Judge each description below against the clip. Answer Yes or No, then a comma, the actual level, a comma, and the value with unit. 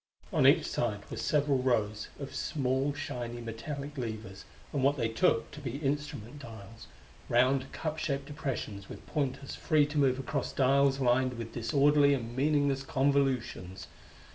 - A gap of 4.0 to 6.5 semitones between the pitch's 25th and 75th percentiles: No, average, 3.3 semitones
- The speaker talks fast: No, average, 150 wpm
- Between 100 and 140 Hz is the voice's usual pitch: Yes, low, 135 Hz